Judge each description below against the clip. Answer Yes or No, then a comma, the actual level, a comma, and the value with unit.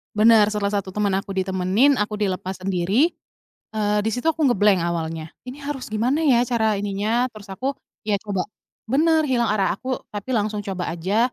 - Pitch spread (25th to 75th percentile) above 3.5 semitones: Yes, average, 4.2 semitones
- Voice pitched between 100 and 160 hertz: No, high, 210 Hz